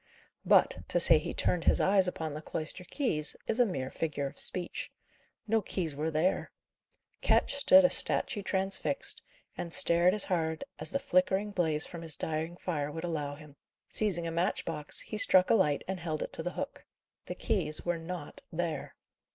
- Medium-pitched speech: Yes, medium, 170 Hz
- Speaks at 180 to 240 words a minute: Yes, average, 185 wpm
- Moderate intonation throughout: Yes, average, 3.4 semitones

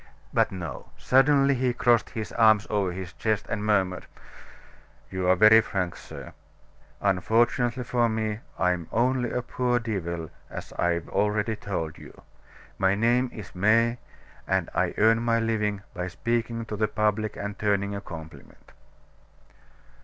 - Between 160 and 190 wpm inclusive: No, average, 145 wpm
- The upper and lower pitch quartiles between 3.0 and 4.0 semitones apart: Yes, average, 3.6 semitones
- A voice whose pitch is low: Yes, low, 105 Hz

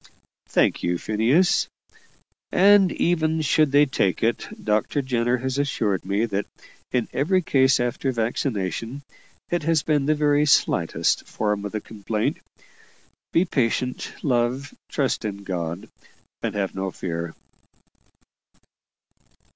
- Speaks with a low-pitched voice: Yes, low, 125 Hz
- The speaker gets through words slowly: Yes, slow, 125 wpm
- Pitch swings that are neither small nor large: No, wide, 5.8 semitones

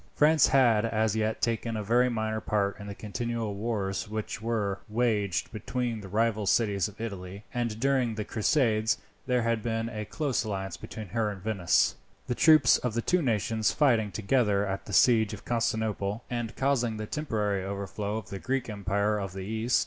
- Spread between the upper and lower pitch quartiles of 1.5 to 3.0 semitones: Yes, narrow, 2.5 semitones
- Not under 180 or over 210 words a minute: Yes, average, 185 wpm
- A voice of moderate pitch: No, low, 110 Hz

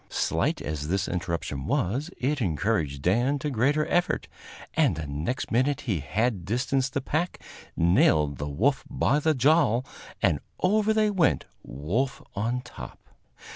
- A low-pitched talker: Yes, low, 120 Hz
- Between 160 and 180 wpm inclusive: No, average, 145 wpm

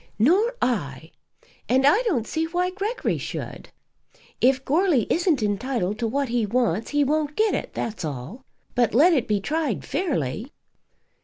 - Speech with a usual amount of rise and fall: No, wide, 7.1 semitones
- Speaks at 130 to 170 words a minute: Yes, average, 155 wpm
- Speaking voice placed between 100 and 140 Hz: No, very high, 265 Hz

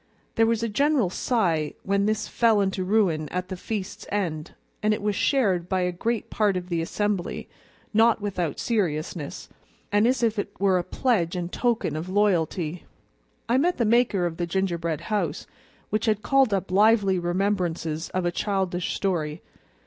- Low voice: No, high, 195 Hz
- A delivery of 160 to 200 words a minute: Yes, average, 170 wpm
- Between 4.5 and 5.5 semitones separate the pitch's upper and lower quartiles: No, average, 3.7 semitones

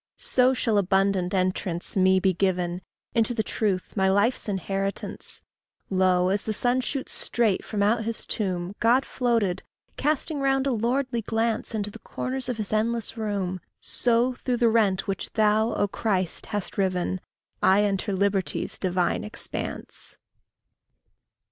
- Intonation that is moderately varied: Yes, average, 3.7 semitones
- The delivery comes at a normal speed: Yes, average, 145 wpm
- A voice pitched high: Yes, high, 205 Hz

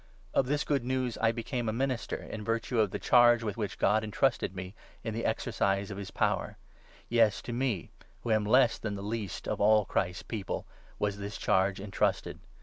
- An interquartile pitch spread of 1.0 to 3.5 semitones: Yes, average, 2.9 semitones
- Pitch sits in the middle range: No, low, 110 Hz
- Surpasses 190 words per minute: Yes, average, 200 wpm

